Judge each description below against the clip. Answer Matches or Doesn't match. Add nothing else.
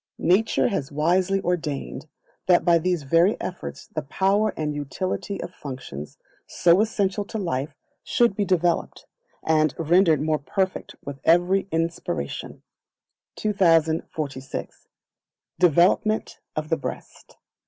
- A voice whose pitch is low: Doesn't match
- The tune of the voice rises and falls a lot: Doesn't match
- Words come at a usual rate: Doesn't match